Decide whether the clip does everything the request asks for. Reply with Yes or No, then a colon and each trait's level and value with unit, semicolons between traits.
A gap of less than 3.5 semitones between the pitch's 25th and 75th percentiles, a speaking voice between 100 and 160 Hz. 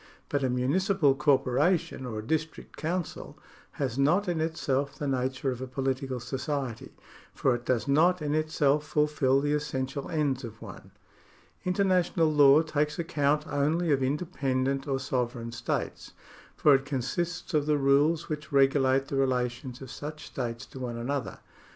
Yes: average, 2.8 semitones; medium, 140 Hz